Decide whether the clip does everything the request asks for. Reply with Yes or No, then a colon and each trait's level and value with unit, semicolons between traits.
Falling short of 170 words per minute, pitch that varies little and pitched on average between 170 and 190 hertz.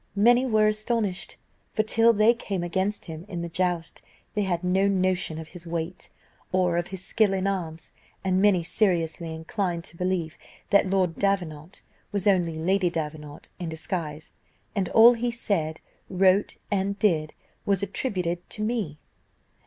No: average, 155 wpm; average, 3.2 semitones; medium, 185 Hz